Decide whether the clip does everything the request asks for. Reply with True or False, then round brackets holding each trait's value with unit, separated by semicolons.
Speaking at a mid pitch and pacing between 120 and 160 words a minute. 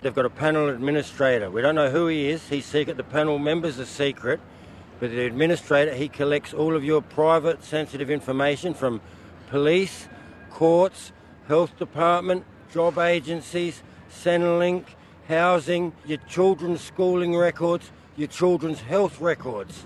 True (155 Hz; 140 wpm)